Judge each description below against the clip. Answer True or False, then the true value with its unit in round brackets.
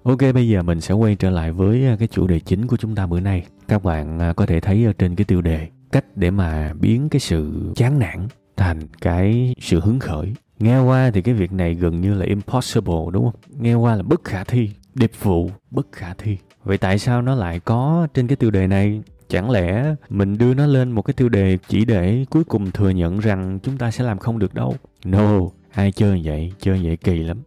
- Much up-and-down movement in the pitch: False (4.7 semitones)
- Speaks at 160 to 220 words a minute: False (230 wpm)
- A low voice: True (100 Hz)